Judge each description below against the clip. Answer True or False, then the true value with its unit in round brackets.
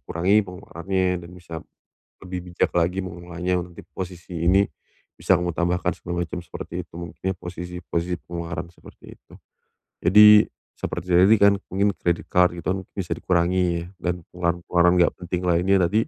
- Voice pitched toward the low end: True (90 Hz)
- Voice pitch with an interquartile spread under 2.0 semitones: True (1.2 semitones)